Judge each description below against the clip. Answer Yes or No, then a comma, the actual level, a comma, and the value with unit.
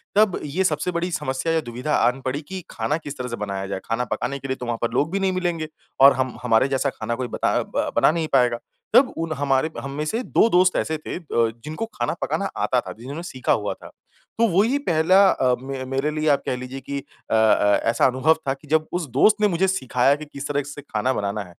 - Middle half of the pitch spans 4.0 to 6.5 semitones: Yes, average, 4.8 semitones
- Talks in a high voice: No, medium, 140 Hz